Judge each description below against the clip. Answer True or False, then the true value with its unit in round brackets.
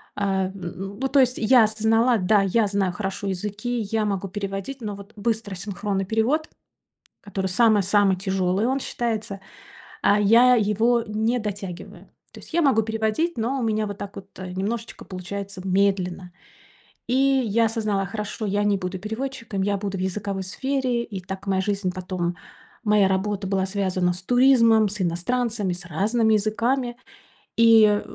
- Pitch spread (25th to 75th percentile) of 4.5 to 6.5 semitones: False (2.9 semitones)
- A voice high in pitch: True (205 Hz)